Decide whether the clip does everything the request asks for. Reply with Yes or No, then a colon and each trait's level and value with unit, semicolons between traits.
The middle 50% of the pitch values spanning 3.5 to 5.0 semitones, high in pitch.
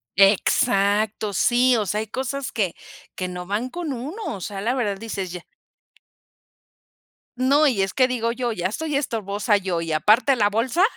Yes: average, 4.5 semitones; high, 220 Hz